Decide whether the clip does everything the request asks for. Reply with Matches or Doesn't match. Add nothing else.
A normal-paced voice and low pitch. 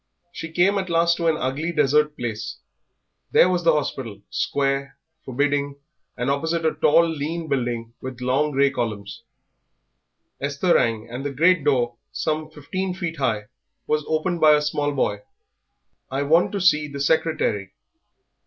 Doesn't match